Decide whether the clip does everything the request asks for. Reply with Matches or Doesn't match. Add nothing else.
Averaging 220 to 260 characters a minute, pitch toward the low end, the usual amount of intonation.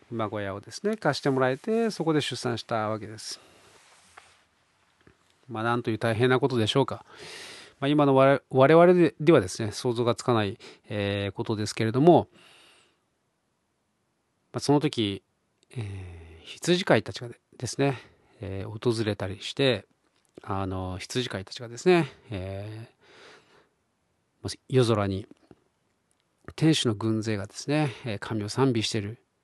Matches